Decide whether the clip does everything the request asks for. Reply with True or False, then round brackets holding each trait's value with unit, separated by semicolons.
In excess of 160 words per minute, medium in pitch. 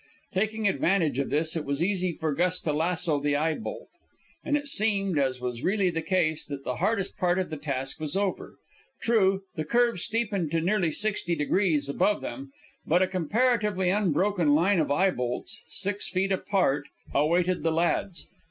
True (180 wpm; 180 Hz)